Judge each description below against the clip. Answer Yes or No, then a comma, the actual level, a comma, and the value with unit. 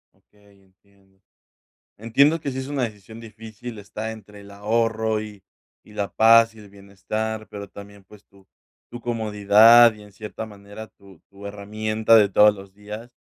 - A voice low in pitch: Yes, low, 105 Hz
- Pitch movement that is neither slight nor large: No, narrow, 1.8 semitones